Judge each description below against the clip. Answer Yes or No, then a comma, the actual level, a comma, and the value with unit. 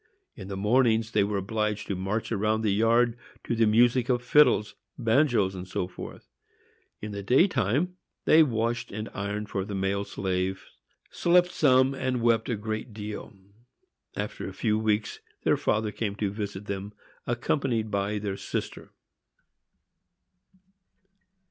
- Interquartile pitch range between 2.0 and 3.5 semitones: Yes, average, 3.0 semitones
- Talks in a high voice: No, low, 110 Hz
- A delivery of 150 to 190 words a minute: No, average, 140 wpm